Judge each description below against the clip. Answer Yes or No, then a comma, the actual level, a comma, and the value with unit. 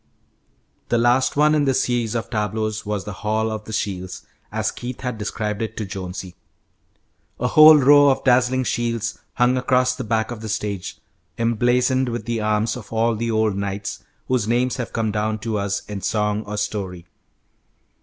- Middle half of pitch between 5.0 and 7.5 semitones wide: No, average, 2.8 semitones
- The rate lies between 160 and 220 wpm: Yes, average, 180 wpm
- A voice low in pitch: Yes, low, 110 Hz